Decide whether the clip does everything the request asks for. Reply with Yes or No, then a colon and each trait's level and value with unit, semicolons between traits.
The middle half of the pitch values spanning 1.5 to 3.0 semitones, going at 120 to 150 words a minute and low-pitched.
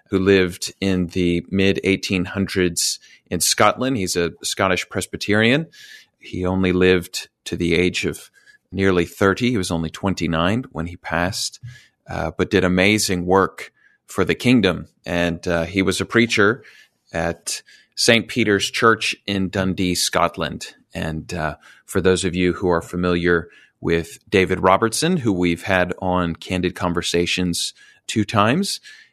Yes: narrow, 2.5 semitones; average, 140 wpm; very low, 95 Hz